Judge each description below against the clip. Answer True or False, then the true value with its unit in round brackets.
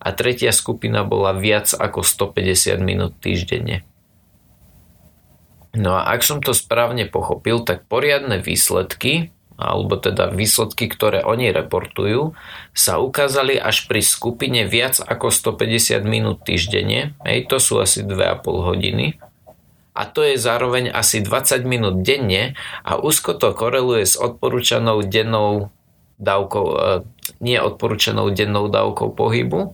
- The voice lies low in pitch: True (110 Hz)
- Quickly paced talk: False (125 wpm)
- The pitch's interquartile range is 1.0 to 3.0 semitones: False (4.1 semitones)